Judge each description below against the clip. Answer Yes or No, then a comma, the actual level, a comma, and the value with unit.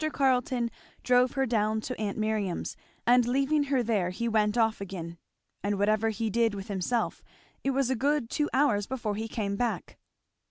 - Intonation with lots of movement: No, average, 3.4 semitones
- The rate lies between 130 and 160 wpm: No, average, 175 wpm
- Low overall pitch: No, high, 225 Hz